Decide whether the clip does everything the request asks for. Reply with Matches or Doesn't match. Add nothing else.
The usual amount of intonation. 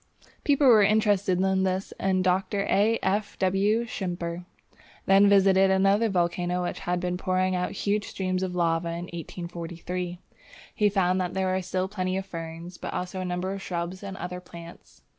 Doesn't match